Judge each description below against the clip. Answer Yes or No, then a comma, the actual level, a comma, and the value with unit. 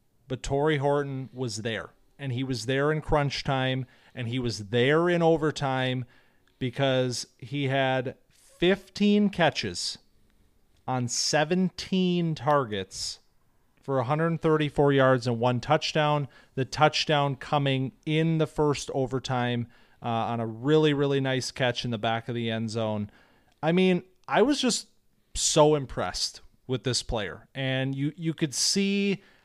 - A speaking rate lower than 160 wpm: Yes, average, 140 wpm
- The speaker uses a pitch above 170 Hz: No, low, 135 Hz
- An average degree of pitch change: Yes, average, 3.9 semitones